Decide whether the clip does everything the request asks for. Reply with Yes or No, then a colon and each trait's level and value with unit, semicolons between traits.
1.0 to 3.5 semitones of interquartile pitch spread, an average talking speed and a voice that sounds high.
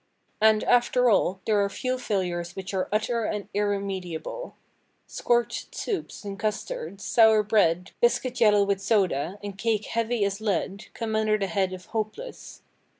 Yes: average, 2.9 semitones; average, 150 wpm; high, 210 Hz